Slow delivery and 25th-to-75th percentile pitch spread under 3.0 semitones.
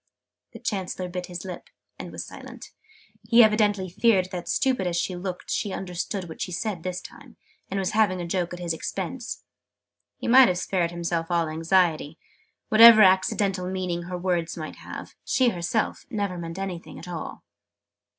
No: average, 170 wpm; narrow, 2.4 semitones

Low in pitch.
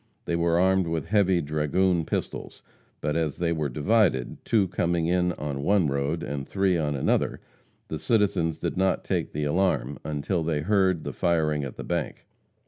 Yes: very low, 85 Hz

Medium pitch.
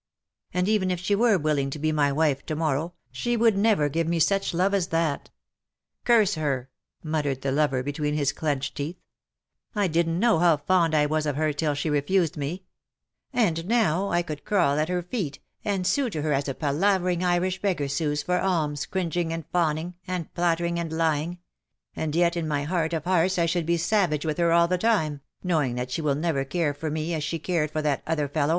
Yes: medium, 165 Hz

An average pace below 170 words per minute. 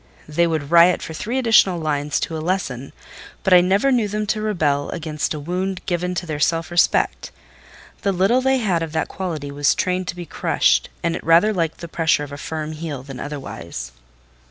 No: average, 200 wpm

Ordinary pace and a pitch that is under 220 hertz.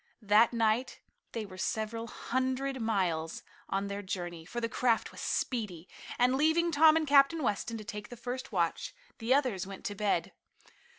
No: average, 170 wpm; high, 225 Hz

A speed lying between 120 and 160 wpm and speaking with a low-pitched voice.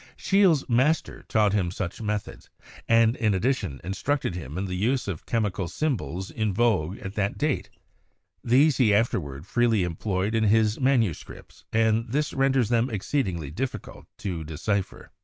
Yes: average, 155 wpm; low, 110 Hz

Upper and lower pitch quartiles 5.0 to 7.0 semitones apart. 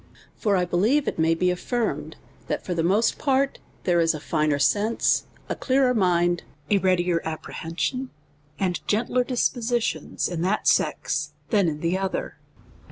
Yes: wide, 5.4 semitones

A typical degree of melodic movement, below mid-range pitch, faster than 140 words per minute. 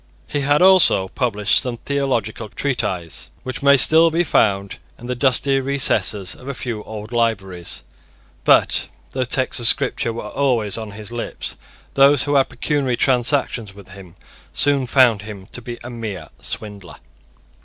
Yes: average, 4.7 semitones; low, 120 Hz; average, 155 wpm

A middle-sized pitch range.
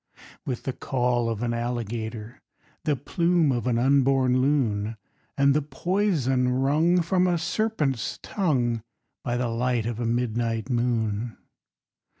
Yes: average, 3.5 semitones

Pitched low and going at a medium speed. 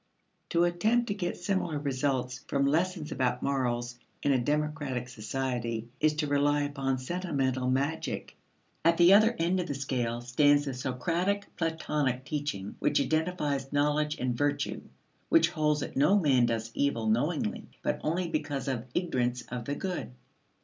No: medium, 145 Hz; average, 155 wpm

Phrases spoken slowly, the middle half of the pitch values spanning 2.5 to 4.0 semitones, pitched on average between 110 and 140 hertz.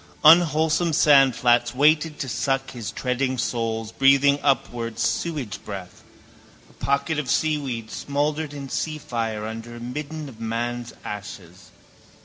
No: slow, 125 wpm; average, 4.4 semitones; low, 135 Hz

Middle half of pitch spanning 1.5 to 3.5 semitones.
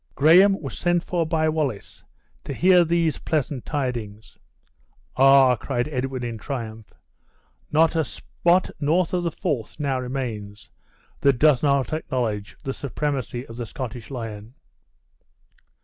No: average, 4.6 semitones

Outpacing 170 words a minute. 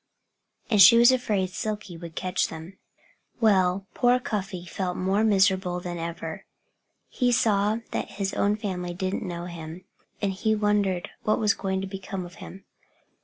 No: average, 160 wpm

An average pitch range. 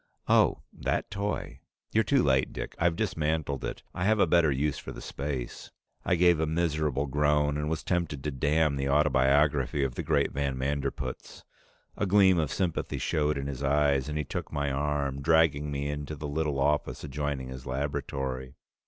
No: narrow, 2.3 semitones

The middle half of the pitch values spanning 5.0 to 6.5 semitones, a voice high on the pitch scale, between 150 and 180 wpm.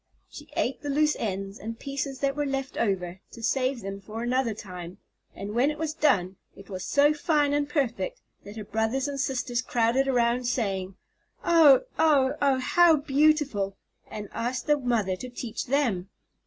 Yes: average, 5.3 semitones; very high, 255 Hz; average, 175 wpm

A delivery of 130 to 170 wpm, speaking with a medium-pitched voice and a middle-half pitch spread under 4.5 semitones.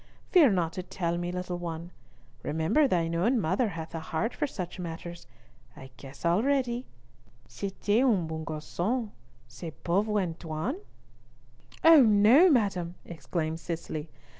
No: slow, 135 wpm; medium, 175 Hz; average, 5.1 semitones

